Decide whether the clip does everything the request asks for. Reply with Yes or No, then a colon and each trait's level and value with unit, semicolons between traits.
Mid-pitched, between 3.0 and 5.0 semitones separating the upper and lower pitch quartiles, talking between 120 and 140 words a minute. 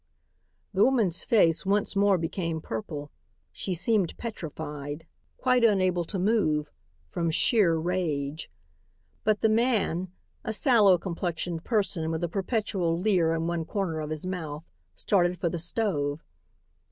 Yes: medium, 175 Hz; average, 4.0 semitones; slow, 135 wpm